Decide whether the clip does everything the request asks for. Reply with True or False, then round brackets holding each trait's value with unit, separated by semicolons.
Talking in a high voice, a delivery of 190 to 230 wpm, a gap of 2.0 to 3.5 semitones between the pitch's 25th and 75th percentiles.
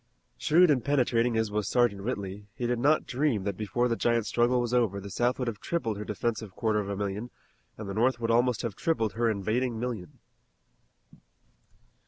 False (115 Hz; 195 wpm; 3.0 semitones)